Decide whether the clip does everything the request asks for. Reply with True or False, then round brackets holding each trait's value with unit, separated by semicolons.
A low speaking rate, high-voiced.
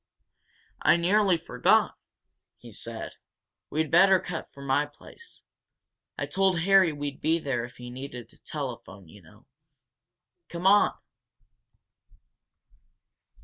False (115 wpm; 160 Hz)